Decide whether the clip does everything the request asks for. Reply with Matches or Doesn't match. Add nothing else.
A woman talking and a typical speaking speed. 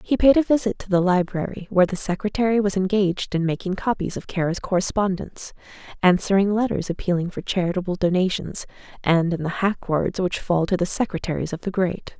Matches